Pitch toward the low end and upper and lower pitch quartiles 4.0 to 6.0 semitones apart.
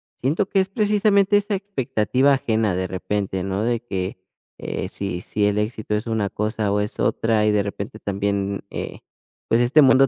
Yes: low, 110 Hz; average, 5.1 semitones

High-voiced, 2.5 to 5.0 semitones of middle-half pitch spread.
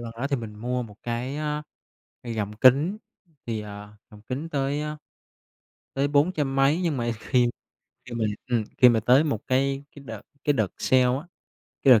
No: low, 130 Hz; average, 3.9 semitones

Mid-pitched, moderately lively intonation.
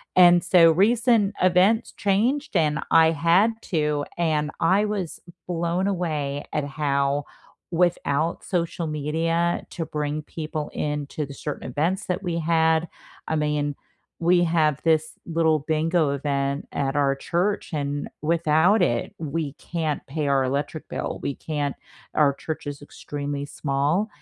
Yes: medium, 160 Hz; average, 3.1 semitones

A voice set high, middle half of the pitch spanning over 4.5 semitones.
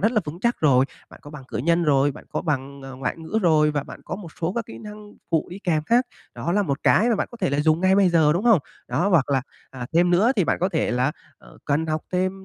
No: medium, 165 Hz; average, 5.0 semitones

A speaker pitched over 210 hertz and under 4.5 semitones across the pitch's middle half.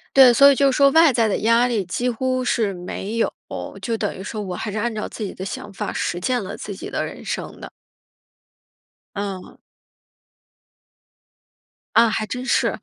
Yes: high, 225 Hz; average, 3.7 semitones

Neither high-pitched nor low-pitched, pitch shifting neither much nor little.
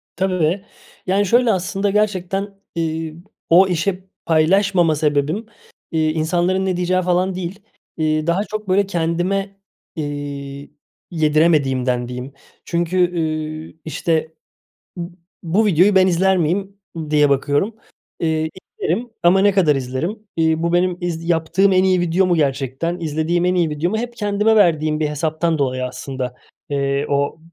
Yes: medium, 170 Hz; average, 3.6 semitones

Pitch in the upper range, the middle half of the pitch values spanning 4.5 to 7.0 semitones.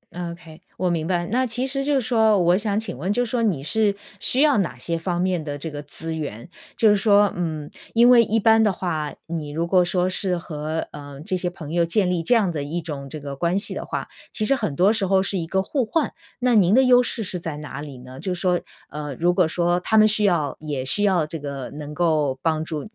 No: medium, 175 Hz; average, 5.3 semitones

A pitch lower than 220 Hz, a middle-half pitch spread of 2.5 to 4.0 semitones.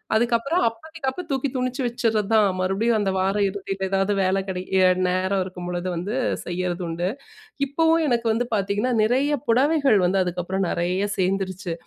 No: high, 200 Hz; average, 4.8 semitones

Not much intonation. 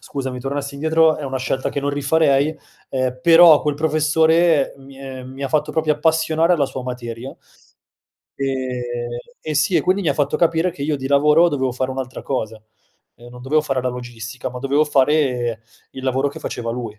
No: average, 3.2 semitones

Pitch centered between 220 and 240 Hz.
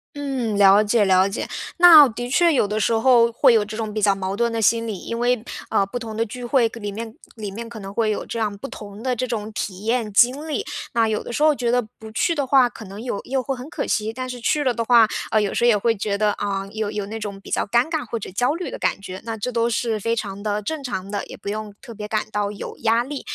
Yes: high, 225 Hz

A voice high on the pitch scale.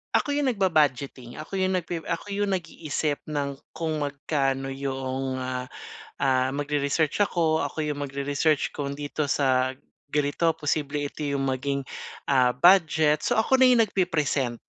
No: medium, 145 Hz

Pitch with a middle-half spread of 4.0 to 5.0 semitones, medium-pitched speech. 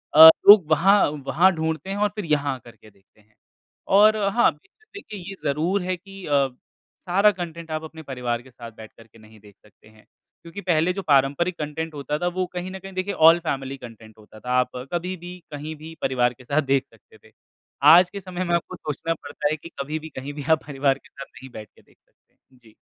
No: wide, 5.5 semitones; medium, 155 Hz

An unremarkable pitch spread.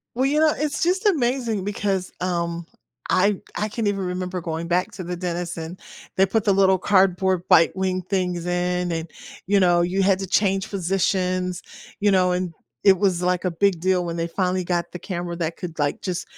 No: narrow, 1.9 semitones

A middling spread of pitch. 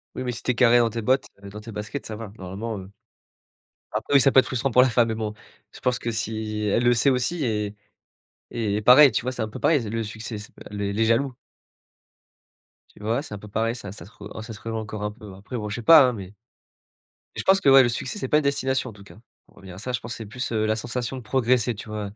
Yes: average, 3.0 semitones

